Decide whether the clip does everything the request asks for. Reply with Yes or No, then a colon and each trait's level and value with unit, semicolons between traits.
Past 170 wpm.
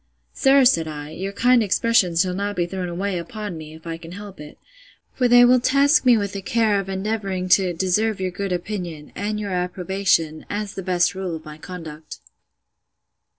Yes: average, 195 wpm